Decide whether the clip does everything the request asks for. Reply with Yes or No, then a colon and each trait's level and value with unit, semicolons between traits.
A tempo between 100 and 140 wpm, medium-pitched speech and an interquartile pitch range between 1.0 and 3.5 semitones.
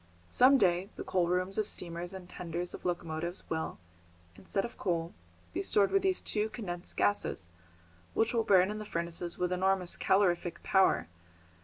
No: average, 170 wpm; medium, 180 Hz; average, 2.9 semitones